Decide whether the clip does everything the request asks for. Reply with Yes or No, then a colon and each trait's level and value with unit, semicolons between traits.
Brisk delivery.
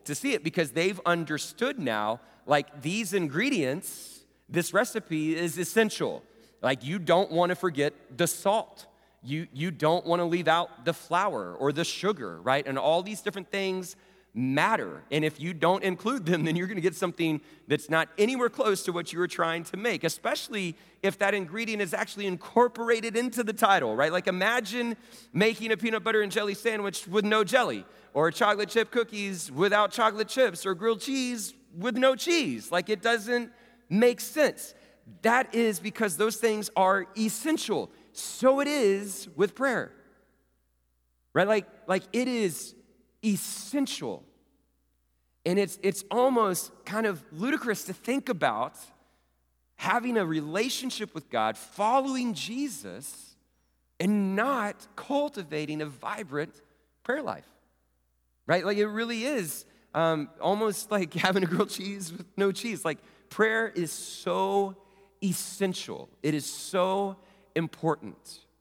No: average, 150 wpm